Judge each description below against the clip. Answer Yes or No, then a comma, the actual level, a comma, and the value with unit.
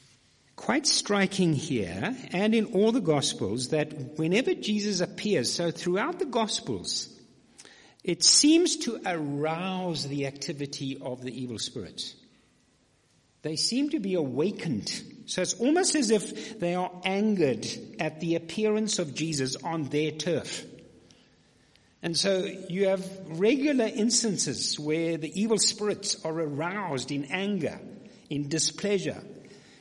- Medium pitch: Yes, medium, 180 Hz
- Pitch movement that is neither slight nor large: No, wide, 5.7 semitones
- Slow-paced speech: Yes, slow, 125 wpm